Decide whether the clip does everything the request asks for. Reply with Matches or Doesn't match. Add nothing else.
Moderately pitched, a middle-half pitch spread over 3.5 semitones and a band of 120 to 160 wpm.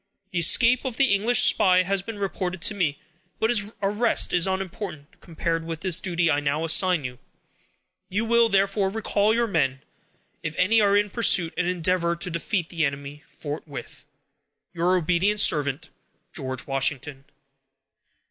Matches